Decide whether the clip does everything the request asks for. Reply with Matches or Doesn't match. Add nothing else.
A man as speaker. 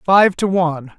Matches